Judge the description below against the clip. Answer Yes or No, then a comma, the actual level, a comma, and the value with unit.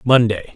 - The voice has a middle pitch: No, low, 115 Hz